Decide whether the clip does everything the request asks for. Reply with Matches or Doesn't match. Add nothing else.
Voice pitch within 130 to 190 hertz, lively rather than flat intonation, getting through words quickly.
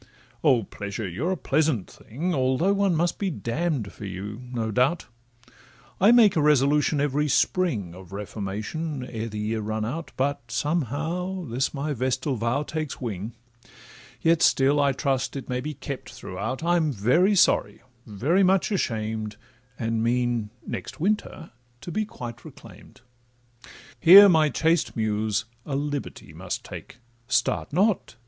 Doesn't match